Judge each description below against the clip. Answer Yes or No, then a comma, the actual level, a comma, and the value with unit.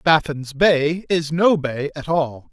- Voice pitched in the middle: Yes, medium, 155 Hz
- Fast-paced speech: No, average, 165 wpm